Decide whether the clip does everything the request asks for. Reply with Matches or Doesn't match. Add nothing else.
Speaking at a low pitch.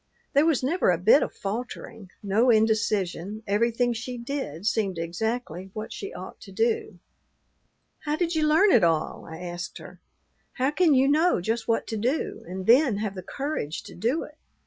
Doesn't match